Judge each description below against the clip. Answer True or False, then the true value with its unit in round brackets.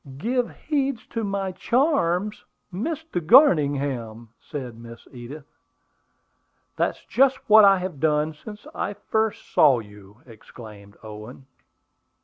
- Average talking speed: False (115 wpm)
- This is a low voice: False (155 Hz)